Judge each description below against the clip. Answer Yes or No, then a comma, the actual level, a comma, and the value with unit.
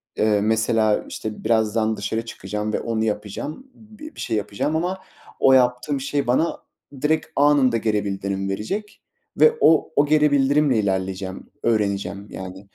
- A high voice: No, low, 110 Hz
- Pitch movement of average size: No, wide, 5.8 semitones